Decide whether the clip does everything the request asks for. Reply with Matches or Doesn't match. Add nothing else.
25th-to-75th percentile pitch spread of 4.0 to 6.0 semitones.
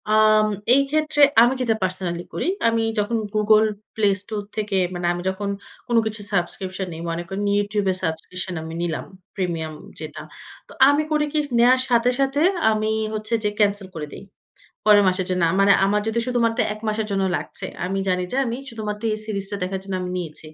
Doesn't match